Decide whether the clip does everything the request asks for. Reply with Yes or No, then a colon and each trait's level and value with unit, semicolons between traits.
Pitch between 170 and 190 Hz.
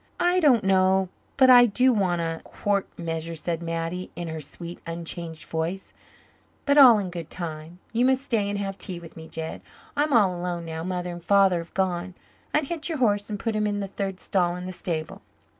Yes: medium, 185 Hz